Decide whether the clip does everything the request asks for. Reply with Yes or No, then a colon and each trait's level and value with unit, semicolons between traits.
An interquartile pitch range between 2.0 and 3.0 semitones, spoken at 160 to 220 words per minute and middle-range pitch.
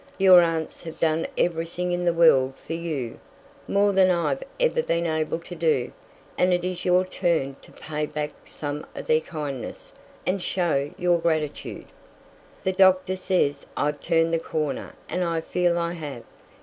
Yes: average, 2.7 semitones; average, 165 wpm; medium, 170 Hz